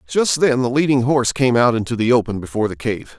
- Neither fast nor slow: No, fast, 245 wpm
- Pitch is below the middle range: Yes, low, 120 Hz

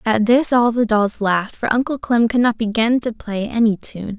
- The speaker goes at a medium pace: No, fast, 230 wpm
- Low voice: No, high, 225 Hz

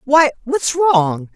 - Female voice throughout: Yes, female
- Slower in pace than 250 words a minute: Yes, slow, 135 wpm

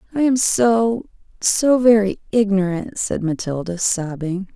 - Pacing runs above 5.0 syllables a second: No, 4.0 syllables/s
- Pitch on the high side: Yes, high, 205 Hz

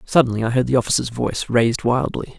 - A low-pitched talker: Yes, low, 120 Hz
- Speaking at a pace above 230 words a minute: No, average, 200 wpm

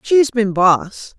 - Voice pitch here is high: Yes, high, 220 Hz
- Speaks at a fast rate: No, average, 150 wpm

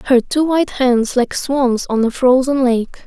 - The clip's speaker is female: Yes, female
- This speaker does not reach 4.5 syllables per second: Yes, 4.3 syllables/s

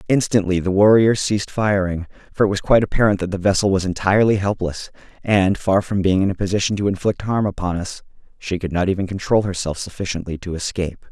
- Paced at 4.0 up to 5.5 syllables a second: No, 6.2 syllables/s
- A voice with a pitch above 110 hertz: No, very low, 95 Hz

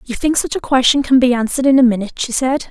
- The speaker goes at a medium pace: No, fast, 290 wpm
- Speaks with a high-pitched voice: Yes, very high, 260 Hz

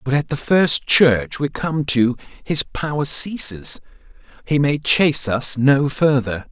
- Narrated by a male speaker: Yes, male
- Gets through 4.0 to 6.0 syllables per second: No, 3.8 syllables/s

